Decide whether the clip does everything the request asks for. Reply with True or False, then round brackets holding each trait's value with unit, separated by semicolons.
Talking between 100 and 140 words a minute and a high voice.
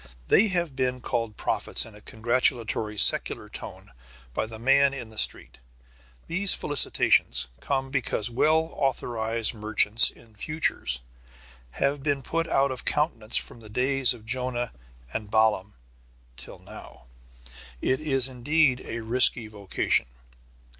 False (135 wpm; 125 Hz)